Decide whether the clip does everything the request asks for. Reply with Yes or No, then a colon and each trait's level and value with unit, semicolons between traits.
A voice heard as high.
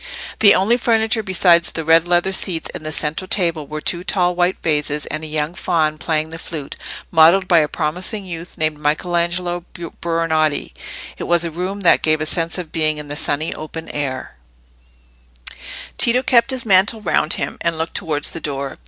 No: medium, 165 Hz